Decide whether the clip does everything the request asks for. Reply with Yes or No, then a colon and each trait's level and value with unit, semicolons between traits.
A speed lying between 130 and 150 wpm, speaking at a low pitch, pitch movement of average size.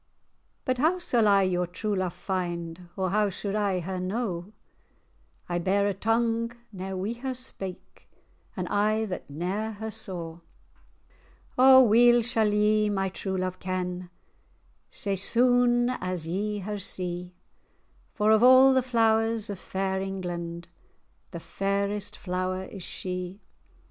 No: average, 140 wpm; high, 195 Hz; average, 3.3 semitones